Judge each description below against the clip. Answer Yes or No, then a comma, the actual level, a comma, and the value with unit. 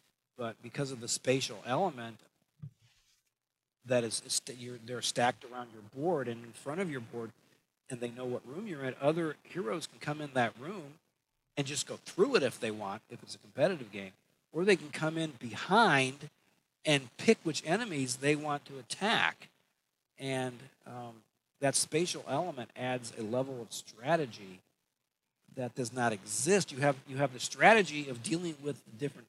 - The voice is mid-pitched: No, low, 130 Hz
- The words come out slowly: No, average, 175 wpm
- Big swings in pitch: No, average, 3.6 semitones